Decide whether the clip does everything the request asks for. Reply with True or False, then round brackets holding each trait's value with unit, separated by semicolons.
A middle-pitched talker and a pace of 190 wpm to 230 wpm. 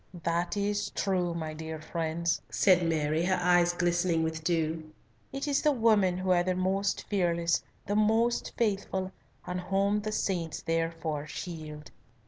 False (175 Hz; 150 wpm)